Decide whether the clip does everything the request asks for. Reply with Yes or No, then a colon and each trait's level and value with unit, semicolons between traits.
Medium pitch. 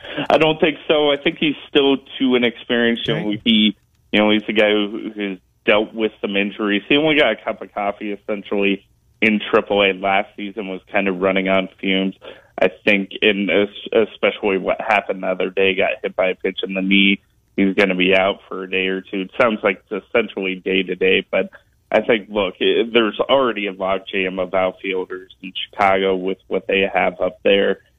No: low, 100 Hz